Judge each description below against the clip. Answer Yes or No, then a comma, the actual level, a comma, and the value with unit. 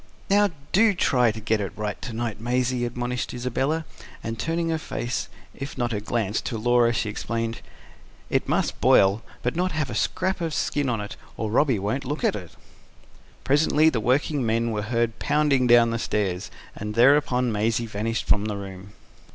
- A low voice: Yes, low, 120 Hz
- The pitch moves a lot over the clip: No, average, 4.0 semitones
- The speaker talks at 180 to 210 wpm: Yes, average, 185 wpm